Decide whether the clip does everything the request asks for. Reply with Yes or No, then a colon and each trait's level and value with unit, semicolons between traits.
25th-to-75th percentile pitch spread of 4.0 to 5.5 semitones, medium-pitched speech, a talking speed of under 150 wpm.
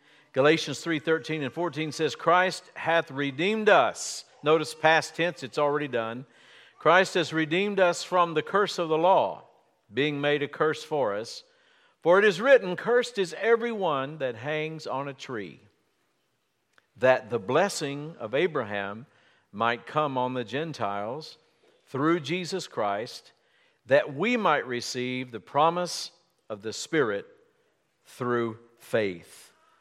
Yes: average, 5.0 semitones; medium, 155 Hz; slow, 135 wpm